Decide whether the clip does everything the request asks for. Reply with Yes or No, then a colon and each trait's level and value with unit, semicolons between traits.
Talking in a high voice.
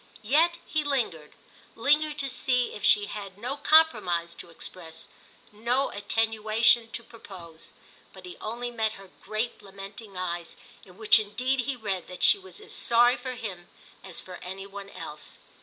Yes: high, 215 Hz